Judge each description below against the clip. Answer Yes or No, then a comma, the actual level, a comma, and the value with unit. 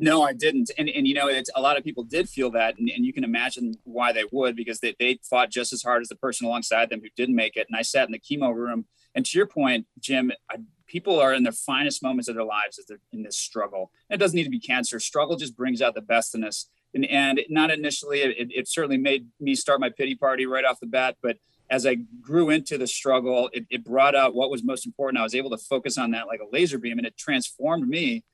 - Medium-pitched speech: No, low, 130 Hz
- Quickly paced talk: Yes, fast, 275 wpm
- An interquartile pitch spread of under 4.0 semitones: Yes, average, 3.5 semitones